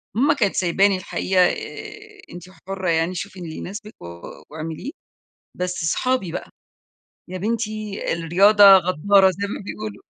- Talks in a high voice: Yes, high, 195 Hz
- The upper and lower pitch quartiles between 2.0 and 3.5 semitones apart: Yes, average, 3.1 semitones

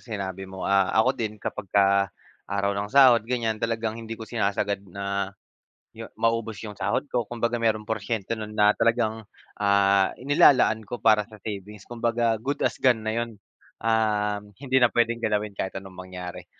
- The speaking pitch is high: No, low, 110 Hz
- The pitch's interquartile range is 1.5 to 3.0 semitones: Yes, narrow, 2.5 semitones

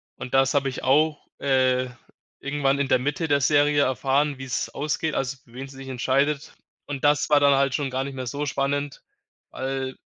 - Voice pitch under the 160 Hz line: Yes, low, 135 Hz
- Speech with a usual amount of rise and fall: No, narrow, 1.5 semitones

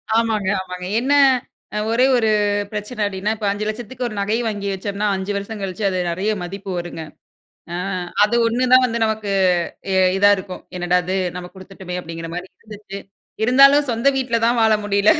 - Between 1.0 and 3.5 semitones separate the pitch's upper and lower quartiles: Yes, average, 3.2 semitones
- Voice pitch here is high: Yes, high, 205 Hz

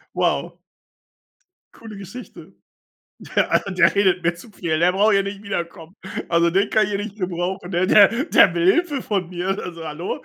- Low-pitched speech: No, high, 190 Hz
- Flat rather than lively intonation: No, average, 3.0 semitones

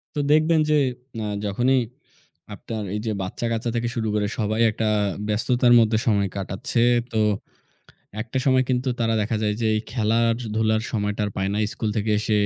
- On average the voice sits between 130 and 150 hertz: No, low, 110 Hz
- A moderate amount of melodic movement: No, narrow, 2.1 semitones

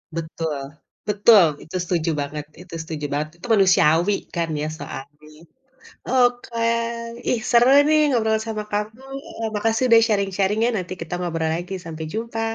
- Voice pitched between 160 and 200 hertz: Yes, high, 190 Hz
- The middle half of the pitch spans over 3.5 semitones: Yes, wide, 5.6 semitones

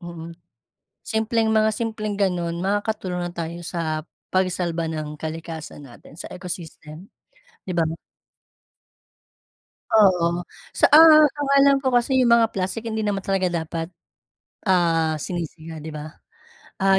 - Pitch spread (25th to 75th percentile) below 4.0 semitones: No, average, 4.8 semitones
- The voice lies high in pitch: No, medium, 180 Hz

